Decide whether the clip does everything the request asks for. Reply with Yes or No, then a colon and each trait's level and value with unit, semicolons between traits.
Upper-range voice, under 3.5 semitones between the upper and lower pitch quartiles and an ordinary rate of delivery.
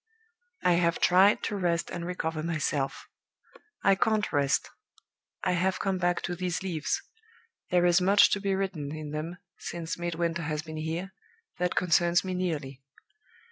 No: medium, 175 Hz; narrow, 2.4 semitones; average, 155 wpm